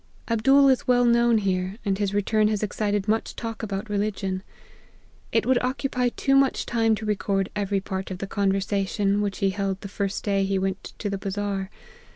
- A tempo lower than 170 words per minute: No, average, 200 wpm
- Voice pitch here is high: Yes, high, 205 Hz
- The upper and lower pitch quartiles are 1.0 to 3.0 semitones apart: Yes, narrow, 2.4 semitones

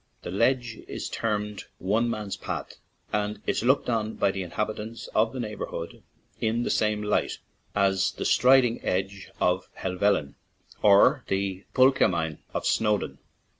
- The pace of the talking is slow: No, average, 165 wpm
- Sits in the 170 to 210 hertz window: No, low, 105 Hz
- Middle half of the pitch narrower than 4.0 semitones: Yes, average, 2.9 semitones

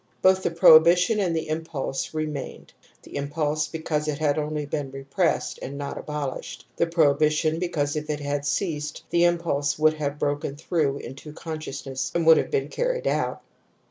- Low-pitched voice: No, medium, 155 Hz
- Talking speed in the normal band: Yes, average, 175 wpm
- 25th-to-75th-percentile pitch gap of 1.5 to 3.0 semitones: Yes, narrow, 2.4 semitones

